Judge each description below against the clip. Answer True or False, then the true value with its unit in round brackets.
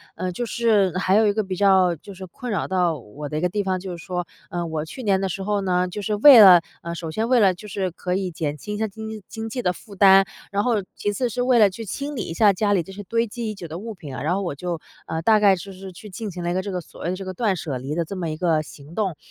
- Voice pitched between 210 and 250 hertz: False (190 Hz)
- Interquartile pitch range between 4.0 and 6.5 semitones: False (3.3 semitones)